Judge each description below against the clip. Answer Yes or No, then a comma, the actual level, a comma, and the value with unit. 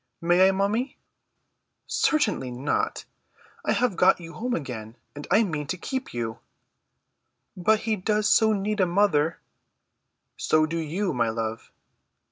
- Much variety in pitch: Yes, wide, 6.3 semitones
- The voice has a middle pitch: Yes, medium, 180 Hz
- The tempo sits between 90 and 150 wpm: Yes, average, 140 wpm